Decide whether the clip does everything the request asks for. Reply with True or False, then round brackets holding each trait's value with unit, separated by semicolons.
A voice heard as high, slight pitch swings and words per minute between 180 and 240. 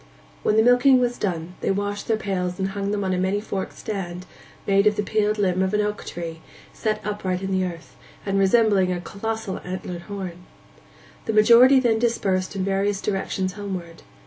True (195 Hz; 2.3 semitones; 190 wpm)